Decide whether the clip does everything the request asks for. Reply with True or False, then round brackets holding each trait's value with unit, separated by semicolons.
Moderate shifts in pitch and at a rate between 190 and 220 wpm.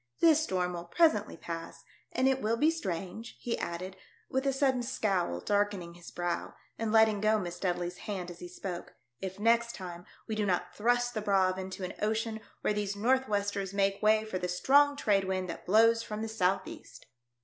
True (3.8 semitones; 200 wpm)